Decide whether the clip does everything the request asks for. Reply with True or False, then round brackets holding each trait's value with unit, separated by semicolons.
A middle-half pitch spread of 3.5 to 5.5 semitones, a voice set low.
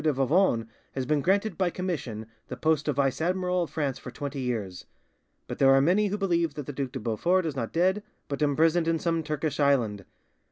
False (4.4 semitones; 150 Hz)